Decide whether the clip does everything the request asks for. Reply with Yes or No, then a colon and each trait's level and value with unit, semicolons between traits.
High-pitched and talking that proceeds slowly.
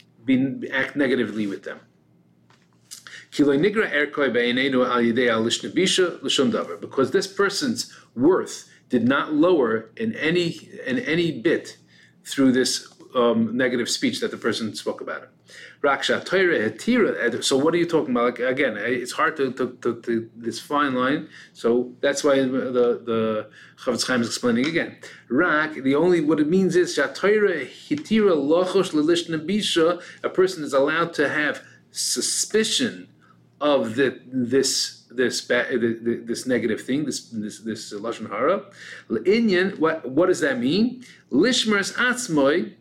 No: medium, 145 Hz; slow, 120 wpm